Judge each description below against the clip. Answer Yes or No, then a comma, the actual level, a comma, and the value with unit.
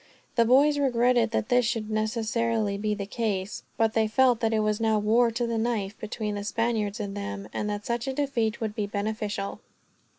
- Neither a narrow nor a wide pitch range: No, narrow, 2.1 semitones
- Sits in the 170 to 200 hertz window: No, high, 220 Hz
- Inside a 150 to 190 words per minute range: No, average, 200 wpm